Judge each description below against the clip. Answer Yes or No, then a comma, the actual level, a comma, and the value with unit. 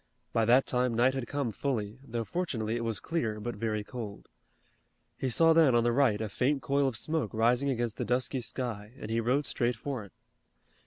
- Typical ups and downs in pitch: Yes, average, 3.3 semitones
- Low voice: Yes, low, 120 Hz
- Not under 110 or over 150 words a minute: No, fast, 205 wpm